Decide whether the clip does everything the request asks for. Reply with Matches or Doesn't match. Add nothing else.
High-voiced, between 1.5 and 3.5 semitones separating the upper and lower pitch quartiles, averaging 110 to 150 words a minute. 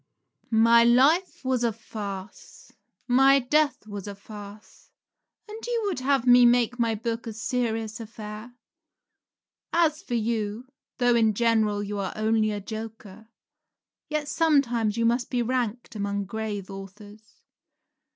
Matches